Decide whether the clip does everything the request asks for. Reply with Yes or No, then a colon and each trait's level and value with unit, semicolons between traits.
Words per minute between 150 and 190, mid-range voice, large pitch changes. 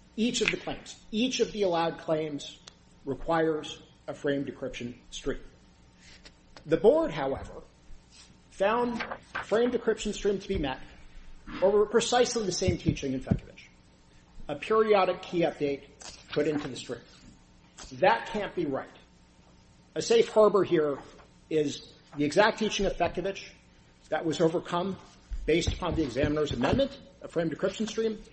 No: average, 140 wpm; medium, 155 Hz; wide, 7.9 semitones